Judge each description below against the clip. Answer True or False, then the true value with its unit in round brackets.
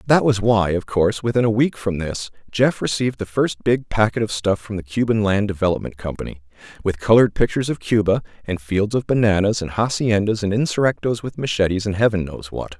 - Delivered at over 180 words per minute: True (200 wpm)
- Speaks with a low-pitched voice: True (105 Hz)